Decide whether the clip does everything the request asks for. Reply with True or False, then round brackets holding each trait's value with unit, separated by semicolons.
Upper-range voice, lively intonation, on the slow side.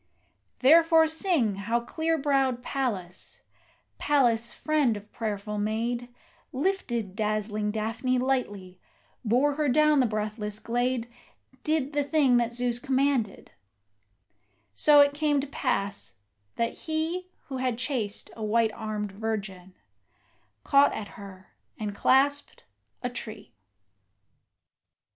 False (240 Hz; 5.0 semitones; 115 wpm)